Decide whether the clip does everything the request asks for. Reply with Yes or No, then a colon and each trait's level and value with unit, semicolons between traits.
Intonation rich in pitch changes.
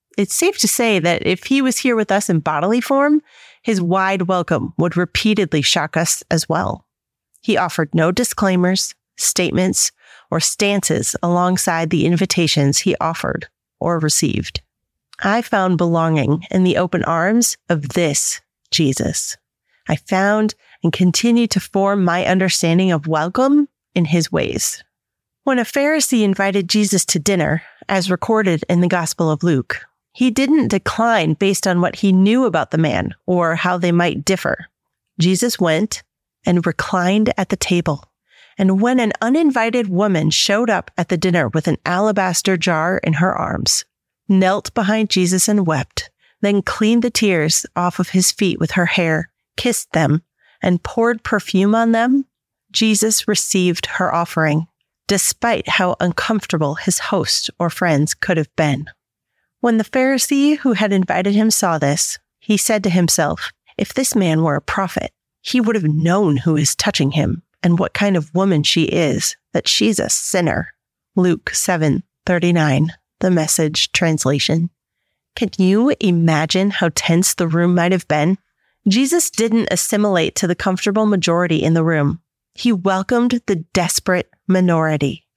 No: average, 4.3 semitones